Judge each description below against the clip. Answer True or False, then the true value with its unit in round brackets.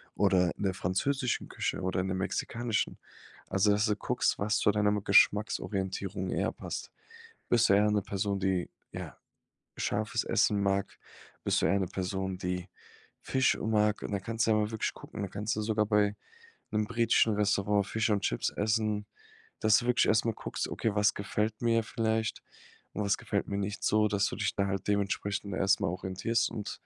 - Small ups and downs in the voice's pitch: True (1.9 semitones)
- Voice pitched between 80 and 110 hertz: True (105 Hz)